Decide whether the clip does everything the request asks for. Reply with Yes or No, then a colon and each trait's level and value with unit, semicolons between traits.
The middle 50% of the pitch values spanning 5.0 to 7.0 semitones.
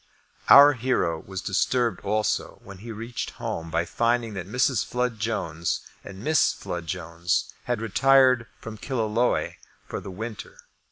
No: average, 4.6 semitones